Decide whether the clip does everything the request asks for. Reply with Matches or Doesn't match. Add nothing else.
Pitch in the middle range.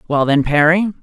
Matches